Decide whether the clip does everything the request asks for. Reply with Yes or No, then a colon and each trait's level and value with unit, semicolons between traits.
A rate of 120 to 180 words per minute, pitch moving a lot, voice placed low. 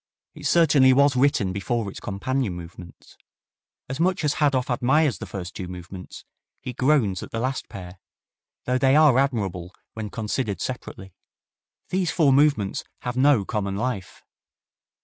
Yes: average, 150 wpm; wide, 6.2 semitones; low, 125 Hz